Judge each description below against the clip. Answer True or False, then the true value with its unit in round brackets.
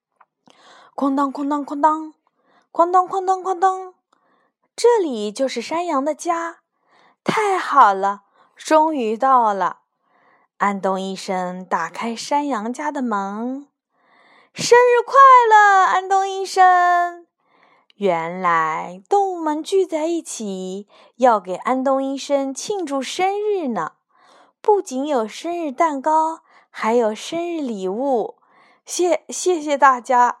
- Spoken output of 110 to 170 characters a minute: True (165 characters per minute)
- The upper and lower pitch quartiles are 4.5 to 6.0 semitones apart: False (7.0 semitones)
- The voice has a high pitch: True (290 Hz)